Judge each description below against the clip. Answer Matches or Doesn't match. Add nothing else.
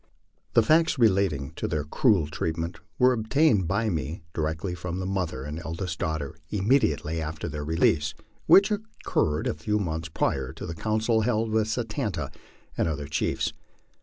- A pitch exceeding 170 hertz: Doesn't match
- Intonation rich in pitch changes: Matches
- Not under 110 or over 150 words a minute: Doesn't match